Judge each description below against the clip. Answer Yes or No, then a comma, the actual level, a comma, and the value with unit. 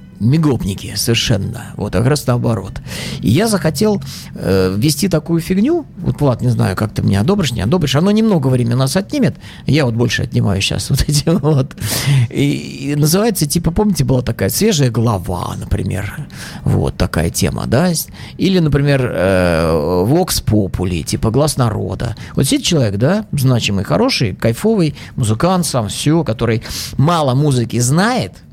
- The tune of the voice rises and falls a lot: Yes, wide, 6.5 semitones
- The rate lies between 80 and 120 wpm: No, average, 155 wpm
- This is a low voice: Yes, low, 130 Hz